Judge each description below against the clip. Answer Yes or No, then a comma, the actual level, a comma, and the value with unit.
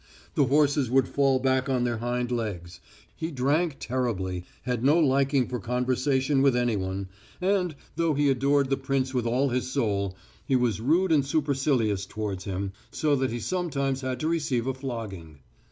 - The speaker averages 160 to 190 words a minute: Yes, average, 170 wpm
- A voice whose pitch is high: No, low, 130 Hz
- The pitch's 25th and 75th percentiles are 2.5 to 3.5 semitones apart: Yes, average, 3.2 semitones